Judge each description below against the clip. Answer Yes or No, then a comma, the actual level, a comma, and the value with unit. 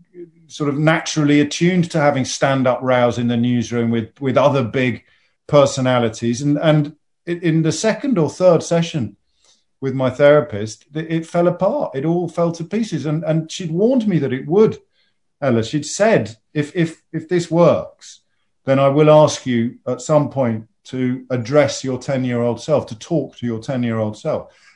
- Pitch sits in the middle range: Yes, medium, 145 Hz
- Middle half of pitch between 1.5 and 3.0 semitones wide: No, average, 4.5 semitones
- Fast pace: No, average, 170 wpm